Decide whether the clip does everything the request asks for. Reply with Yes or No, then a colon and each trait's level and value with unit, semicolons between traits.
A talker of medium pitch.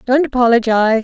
No: high, 240 Hz